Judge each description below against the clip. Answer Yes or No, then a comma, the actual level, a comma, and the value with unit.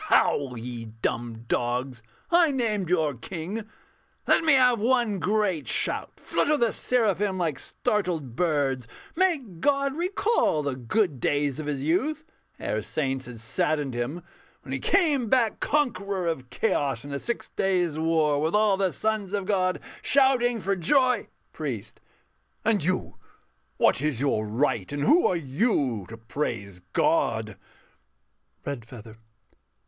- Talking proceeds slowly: No, average, 145 wpm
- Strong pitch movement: Yes, wide, 8.8 semitones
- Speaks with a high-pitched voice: No, medium, 170 Hz